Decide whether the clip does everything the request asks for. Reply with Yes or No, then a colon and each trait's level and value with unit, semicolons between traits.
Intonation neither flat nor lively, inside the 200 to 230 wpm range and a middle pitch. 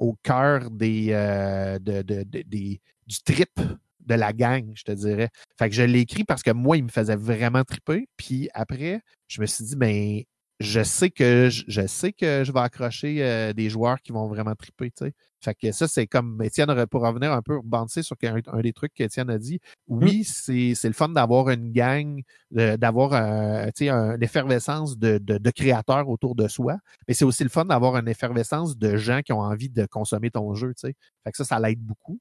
No: average, 3.8 semitones; fast, 220 wpm; low, 120 Hz